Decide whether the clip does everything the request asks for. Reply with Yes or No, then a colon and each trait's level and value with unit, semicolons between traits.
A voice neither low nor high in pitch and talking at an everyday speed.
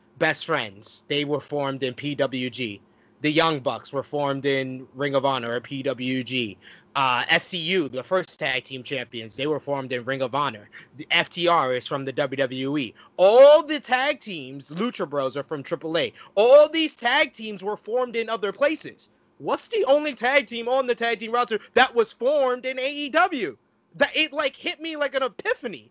Yes: medium, 165 Hz; average, 185 wpm